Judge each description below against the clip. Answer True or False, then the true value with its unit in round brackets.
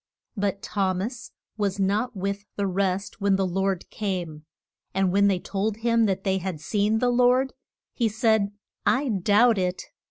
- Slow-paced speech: False (165 wpm)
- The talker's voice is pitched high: True (200 Hz)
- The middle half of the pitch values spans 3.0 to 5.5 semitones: False (2.4 semitones)